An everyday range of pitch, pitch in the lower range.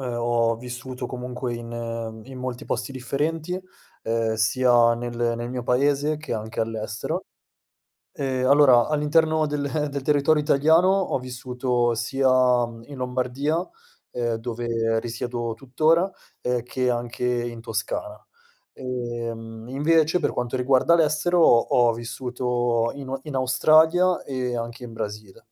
Yes: average, 3.1 semitones; low, 125 Hz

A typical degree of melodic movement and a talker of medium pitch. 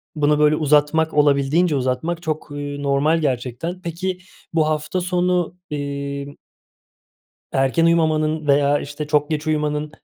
No: narrow, 2.2 semitones; medium, 150 Hz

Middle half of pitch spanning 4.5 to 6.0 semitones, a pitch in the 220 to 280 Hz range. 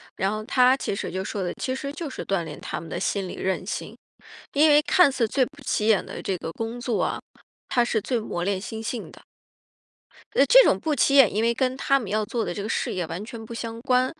Yes: average, 4.8 semitones; high, 230 Hz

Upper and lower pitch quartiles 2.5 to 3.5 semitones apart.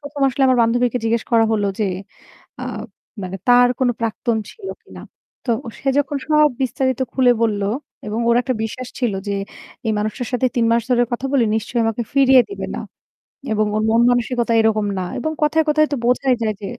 Yes: average, 2.9 semitones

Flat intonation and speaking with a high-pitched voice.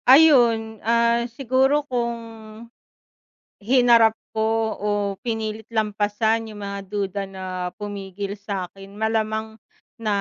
Yes: narrow, 2.1 semitones; high, 220 Hz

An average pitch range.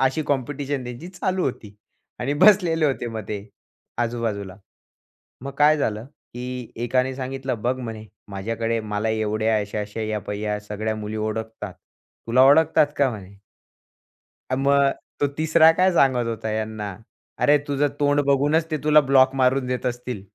Yes: average, 4.5 semitones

